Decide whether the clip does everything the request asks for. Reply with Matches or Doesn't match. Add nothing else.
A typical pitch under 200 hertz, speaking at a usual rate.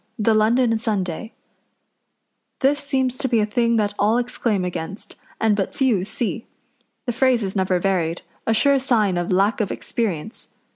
Doesn't match